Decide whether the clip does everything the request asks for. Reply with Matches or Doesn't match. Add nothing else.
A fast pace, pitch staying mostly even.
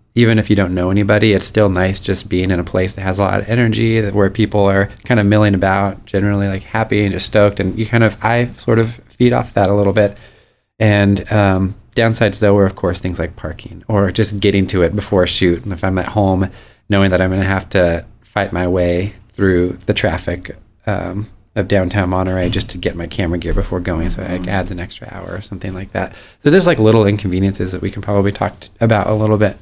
Matches